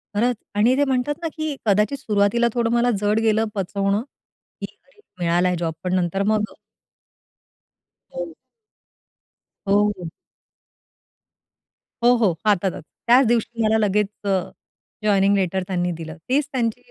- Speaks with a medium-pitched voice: No, high, 210 Hz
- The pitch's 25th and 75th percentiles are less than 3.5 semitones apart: No, average, 3.8 semitones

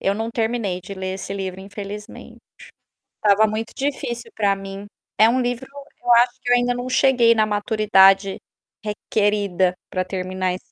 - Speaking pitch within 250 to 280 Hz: No, high, 210 Hz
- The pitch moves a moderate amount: Yes, average, 3.6 semitones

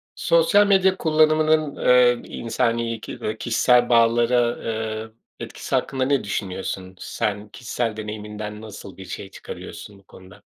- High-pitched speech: No, low, 115 Hz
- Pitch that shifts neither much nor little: Yes, average, 3.5 semitones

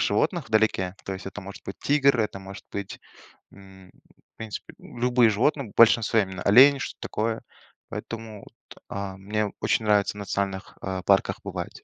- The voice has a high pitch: No, low, 105 Hz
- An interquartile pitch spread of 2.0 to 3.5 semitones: Yes, average, 2.7 semitones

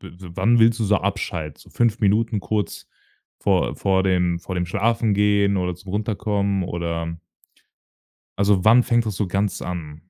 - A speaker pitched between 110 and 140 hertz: No, low, 100 Hz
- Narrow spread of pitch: No, average, 3.2 semitones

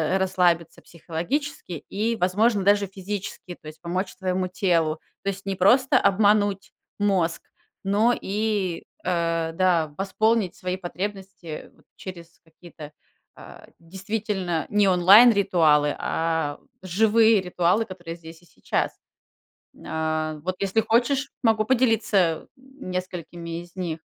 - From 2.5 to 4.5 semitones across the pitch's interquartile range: Yes, average, 3.5 semitones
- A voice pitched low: No, medium, 185 Hz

